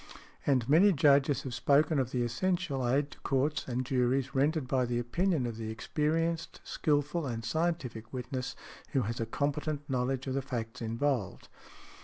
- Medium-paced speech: Yes, average, 165 wpm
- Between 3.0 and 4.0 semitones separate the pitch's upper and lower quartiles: Yes, average, 3.5 semitones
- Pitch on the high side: No, low, 135 Hz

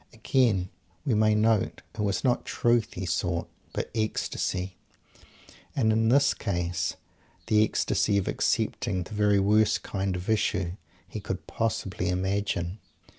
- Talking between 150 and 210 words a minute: No, slow, 135 wpm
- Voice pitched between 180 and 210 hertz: No, low, 100 Hz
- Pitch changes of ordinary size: Yes, average, 3.1 semitones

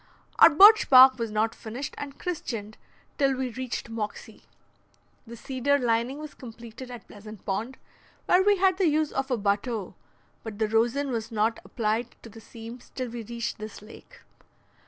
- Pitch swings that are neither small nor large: Yes, average, 3.5 semitones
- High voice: Yes, high, 235 Hz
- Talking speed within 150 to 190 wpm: Yes, average, 170 wpm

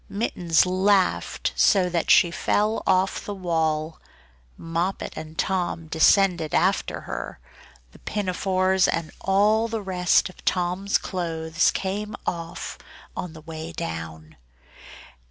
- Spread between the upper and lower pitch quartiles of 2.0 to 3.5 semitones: Yes, average, 2.9 semitones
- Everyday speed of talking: No, slow, 120 wpm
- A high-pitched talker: No, medium, 180 Hz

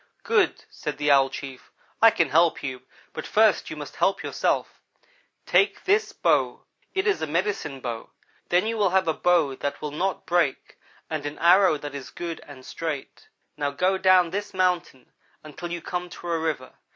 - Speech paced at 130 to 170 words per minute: No, average, 185 wpm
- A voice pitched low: No, medium, 170 Hz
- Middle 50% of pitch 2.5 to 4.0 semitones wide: No, average, 4.5 semitones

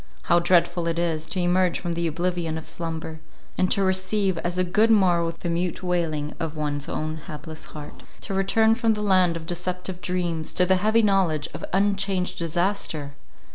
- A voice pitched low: No, medium, 175 Hz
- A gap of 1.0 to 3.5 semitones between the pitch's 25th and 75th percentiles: Yes, narrow, 2.4 semitones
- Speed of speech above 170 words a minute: Yes, average, 180 wpm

